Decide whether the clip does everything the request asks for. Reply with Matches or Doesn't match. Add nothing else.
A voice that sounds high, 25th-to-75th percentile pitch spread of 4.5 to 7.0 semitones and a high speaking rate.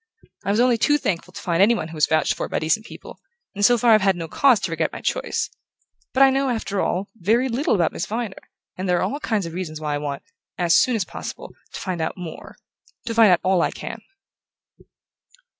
Matches